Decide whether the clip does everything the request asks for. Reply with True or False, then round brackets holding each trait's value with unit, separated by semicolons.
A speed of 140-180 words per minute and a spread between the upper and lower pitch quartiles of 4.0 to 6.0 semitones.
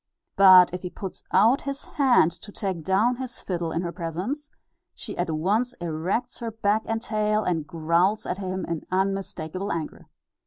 True (170 wpm; 4.4 semitones)